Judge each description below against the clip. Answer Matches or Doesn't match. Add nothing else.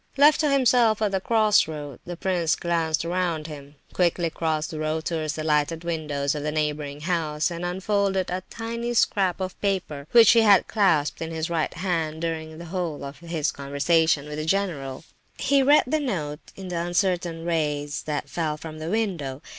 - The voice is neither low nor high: Matches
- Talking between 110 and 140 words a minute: Doesn't match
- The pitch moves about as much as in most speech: Matches